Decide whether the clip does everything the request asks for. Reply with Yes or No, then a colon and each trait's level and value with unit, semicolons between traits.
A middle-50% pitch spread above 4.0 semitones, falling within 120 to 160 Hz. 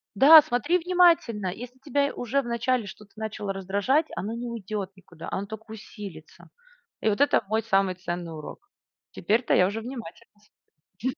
No: average, 4.6 semitones; high, 220 Hz